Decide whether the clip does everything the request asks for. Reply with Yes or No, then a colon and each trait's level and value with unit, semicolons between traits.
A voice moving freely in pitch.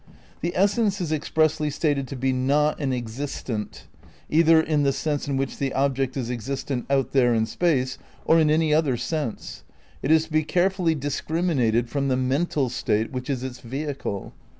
No: average, 3.6 semitones